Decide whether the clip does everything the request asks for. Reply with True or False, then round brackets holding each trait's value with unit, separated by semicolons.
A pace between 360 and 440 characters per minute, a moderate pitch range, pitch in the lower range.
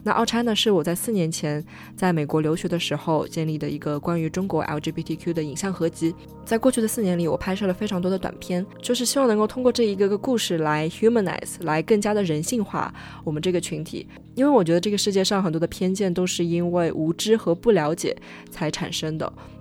False (365 characters per minute; 4.7 semitones; 175 Hz)